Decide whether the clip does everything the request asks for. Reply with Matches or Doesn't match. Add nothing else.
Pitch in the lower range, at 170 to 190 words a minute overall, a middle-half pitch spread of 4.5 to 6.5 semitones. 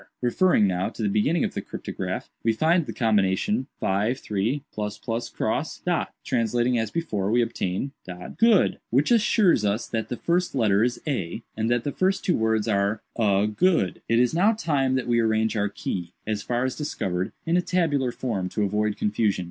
Matches